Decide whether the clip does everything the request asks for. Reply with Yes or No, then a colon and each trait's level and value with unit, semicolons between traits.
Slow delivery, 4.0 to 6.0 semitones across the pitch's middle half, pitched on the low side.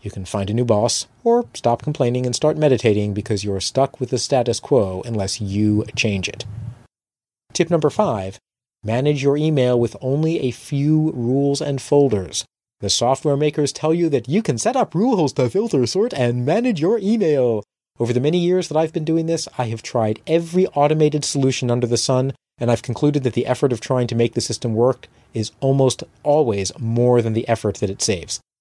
No: average, 200 wpm; average, 4.6 semitones; low, 125 Hz